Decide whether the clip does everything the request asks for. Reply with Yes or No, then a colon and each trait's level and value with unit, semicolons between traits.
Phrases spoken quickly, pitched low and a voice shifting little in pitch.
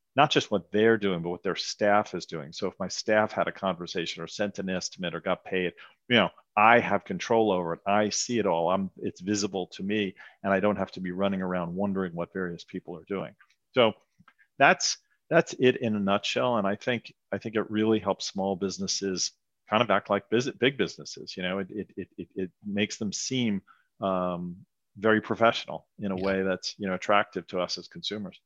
Yes: fast, 215 wpm; low, 100 Hz; narrow, 2.2 semitones